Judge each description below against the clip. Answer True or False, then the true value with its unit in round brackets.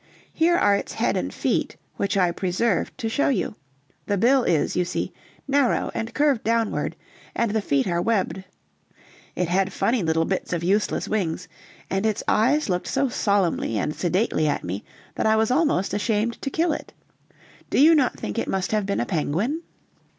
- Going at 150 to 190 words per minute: True (185 wpm)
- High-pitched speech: True (205 Hz)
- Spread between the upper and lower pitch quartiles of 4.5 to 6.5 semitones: True (4.9 semitones)